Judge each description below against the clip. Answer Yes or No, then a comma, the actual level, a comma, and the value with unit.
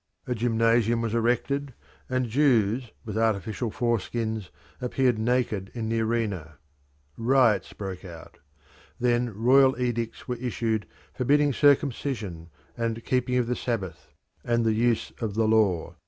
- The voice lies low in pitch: Yes, low, 115 Hz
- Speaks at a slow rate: Yes, slow, 130 wpm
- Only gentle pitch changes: Yes, narrow, 2.3 semitones